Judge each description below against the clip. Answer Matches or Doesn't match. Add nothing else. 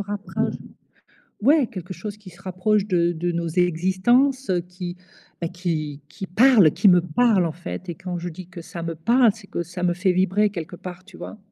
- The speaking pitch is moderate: Matches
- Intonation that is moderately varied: Matches